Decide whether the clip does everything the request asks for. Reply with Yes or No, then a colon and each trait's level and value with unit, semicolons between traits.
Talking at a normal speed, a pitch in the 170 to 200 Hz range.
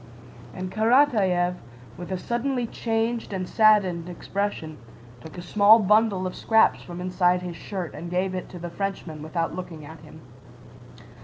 Yes: average, 155 wpm; medium, 185 Hz